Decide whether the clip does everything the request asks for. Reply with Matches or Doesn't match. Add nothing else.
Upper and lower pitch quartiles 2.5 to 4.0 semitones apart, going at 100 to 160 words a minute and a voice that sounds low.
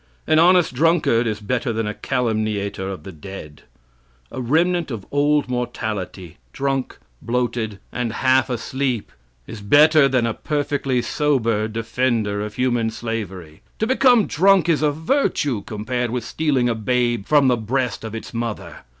Doesn't match